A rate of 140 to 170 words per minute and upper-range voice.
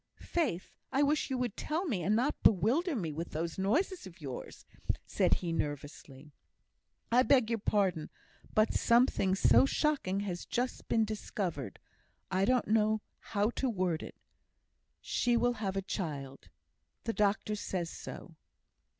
Yes: average, 150 wpm; high, 205 Hz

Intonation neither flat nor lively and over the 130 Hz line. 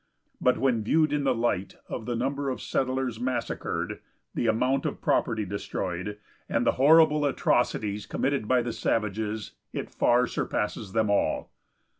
No: average, 3.9 semitones; low, 120 Hz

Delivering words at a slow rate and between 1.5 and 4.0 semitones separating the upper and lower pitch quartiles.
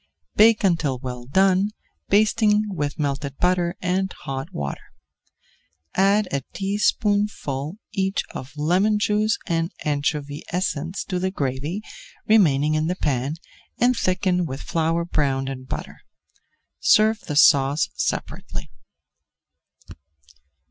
No: slow, 115 wpm; wide, 5.6 semitones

